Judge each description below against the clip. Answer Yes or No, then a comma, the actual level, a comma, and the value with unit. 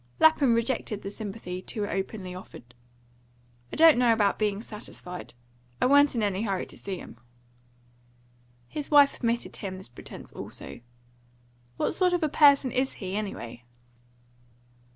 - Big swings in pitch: Yes, wide, 5.9 semitones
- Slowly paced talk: No, average, 145 wpm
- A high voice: Yes, high, 215 Hz